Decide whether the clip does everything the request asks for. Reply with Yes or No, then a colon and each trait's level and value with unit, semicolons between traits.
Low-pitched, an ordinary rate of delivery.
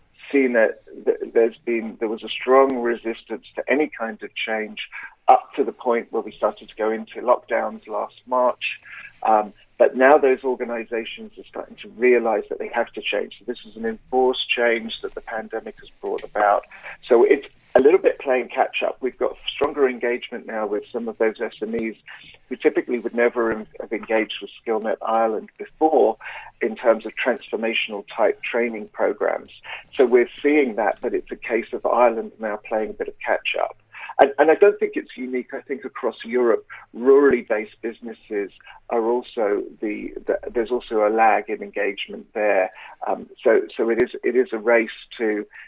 Yes: low, 130 Hz; average, 185 wpm